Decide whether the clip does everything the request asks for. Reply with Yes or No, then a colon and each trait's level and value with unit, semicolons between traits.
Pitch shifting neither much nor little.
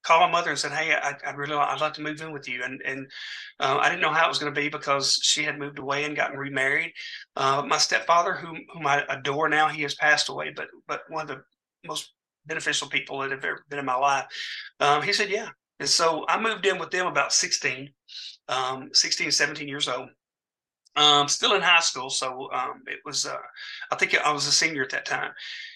No: narrow, 1.8 semitones